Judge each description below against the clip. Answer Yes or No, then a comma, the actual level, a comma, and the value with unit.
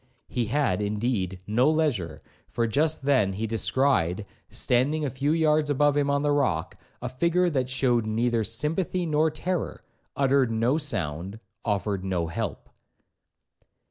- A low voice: Yes, low, 130 Hz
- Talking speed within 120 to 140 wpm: Yes, slow, 135 wpm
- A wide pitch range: Yes, wide, 5.8 semitones